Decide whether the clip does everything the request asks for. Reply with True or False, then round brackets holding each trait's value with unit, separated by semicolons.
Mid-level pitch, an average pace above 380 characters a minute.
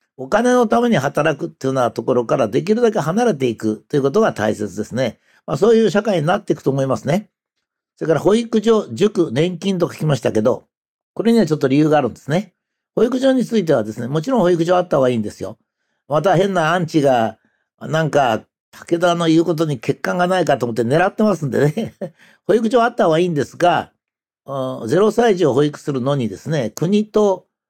True (165 Hz; 420 characters per minute)